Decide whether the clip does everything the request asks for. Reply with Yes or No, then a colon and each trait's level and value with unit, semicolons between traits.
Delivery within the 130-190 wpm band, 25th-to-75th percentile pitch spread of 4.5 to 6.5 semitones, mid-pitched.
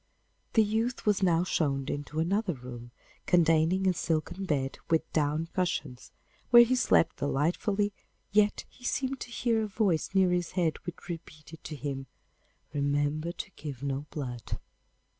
Yes: average, 150 wpm; average, 5.3 semitones; medium, 165 Hz